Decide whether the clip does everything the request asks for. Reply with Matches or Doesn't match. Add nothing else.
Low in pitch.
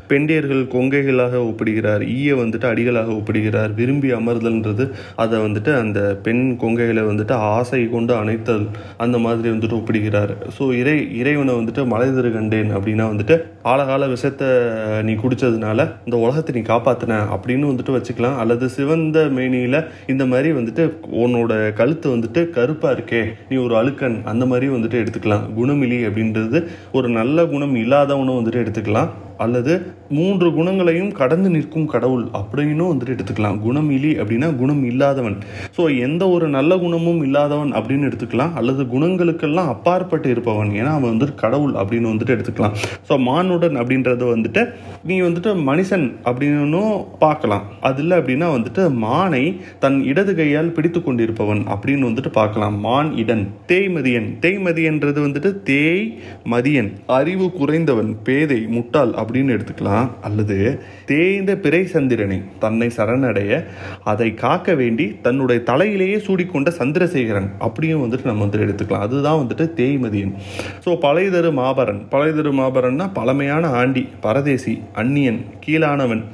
Matches